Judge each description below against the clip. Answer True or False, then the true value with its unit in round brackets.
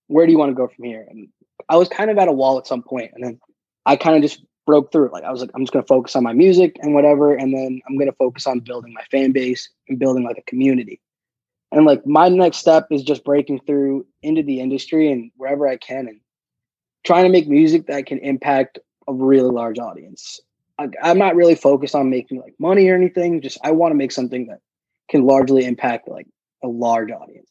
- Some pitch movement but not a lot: True (3.4 semitones)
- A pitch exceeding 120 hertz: True (135 Hz)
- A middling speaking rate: False (240 wpm)